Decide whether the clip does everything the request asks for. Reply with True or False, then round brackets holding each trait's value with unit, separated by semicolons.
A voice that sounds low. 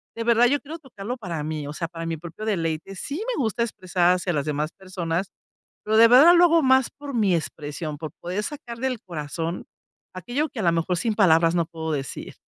False (185 Hz)